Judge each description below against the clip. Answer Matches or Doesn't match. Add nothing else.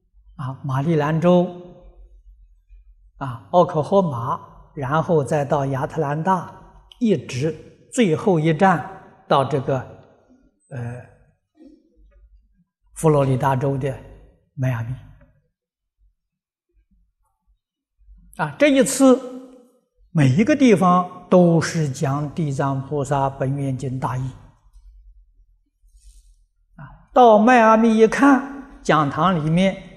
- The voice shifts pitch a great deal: Matches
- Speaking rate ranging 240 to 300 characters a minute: Doesn't match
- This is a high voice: Doesn't match